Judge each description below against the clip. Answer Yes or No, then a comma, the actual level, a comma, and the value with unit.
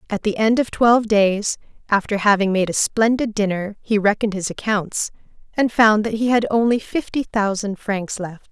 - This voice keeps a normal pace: Yes, average, 185 wpm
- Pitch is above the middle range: Yes, high, 210 Hz